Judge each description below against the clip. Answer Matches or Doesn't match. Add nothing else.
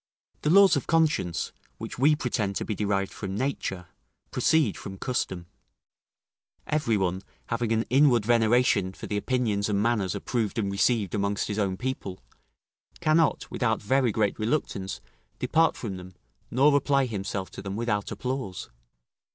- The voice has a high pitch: Doesn't match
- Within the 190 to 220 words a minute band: Doesn't match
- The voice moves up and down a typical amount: Matches